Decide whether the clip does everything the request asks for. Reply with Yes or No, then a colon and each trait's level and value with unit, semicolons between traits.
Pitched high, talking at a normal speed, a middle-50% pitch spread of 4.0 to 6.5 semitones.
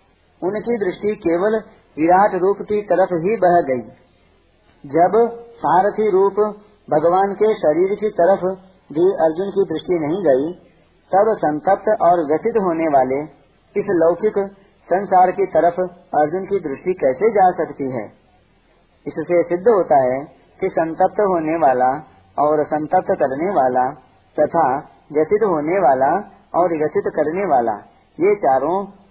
No: medium, 180 Hz; average, 130 wpm; average, 4.8 semitones